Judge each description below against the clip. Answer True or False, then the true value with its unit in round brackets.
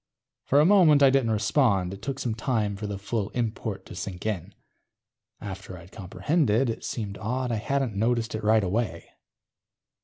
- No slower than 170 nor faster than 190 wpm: True (175 wpm)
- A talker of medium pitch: False (110 Hz)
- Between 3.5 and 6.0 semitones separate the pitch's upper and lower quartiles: True (4.1 semitones)